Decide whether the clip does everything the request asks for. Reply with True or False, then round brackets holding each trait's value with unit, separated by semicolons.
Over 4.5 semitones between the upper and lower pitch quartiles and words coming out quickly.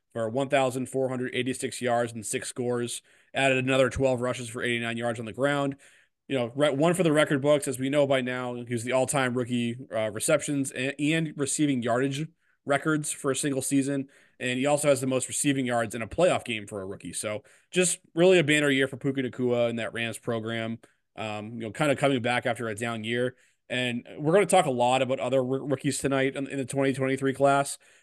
False (2.6 semitones; 210 wpm)